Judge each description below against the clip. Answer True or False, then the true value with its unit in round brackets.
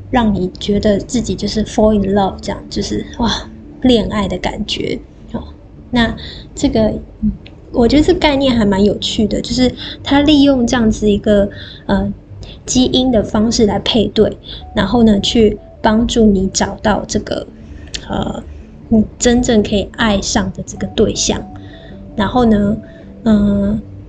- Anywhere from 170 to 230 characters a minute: True (225 characters per minute)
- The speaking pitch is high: True (215 Hz)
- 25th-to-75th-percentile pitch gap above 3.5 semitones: False (3.0 semitones)